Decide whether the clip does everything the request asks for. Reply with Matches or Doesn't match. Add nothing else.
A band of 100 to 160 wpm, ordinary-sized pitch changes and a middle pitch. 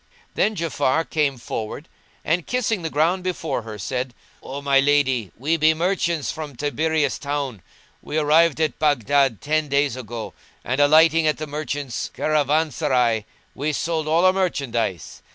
Matches